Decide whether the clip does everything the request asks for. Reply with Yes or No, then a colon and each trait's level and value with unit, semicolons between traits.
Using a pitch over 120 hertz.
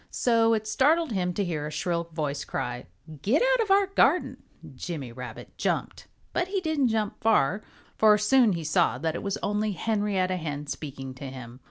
Yes: high, 190 Hz